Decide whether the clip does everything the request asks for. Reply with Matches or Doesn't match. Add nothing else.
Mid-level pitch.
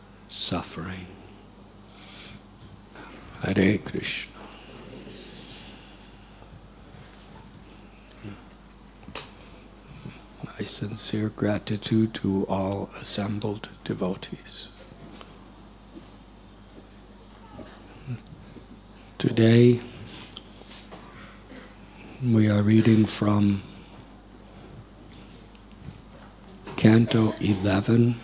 Doesn't match